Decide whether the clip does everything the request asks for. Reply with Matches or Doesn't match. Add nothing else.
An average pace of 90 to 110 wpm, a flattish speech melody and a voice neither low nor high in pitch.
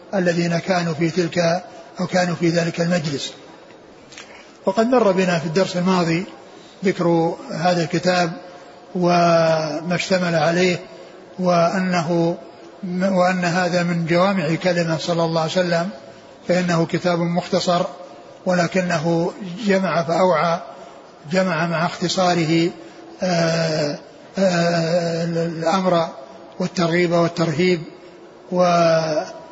Matches